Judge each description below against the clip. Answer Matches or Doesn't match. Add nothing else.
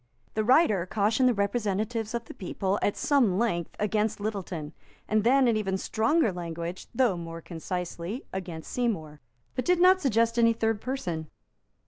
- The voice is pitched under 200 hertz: Doesn't match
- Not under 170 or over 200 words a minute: Doesn't match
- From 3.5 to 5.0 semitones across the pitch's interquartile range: Matches